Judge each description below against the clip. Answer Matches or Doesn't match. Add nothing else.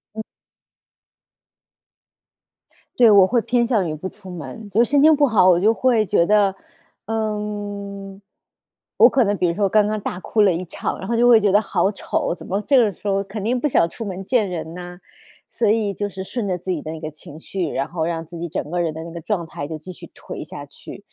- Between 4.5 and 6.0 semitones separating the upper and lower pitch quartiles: Doesn't match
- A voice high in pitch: Matches